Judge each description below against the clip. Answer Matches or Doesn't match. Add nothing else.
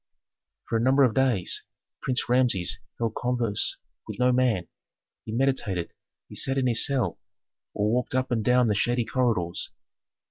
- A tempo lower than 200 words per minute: Matches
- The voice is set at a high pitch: Doesn't match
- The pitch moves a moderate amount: Matches